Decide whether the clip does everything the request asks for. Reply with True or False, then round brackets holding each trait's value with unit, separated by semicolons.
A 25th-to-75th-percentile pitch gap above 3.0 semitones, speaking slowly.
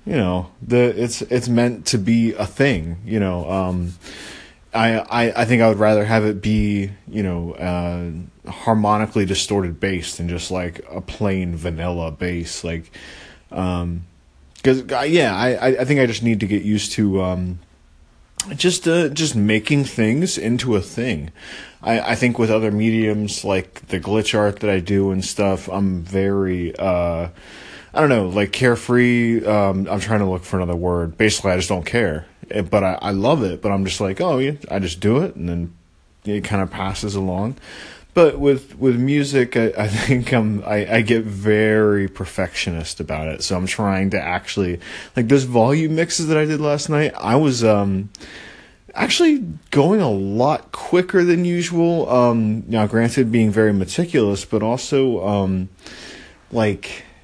False (4.6 semitones; 175 wpm)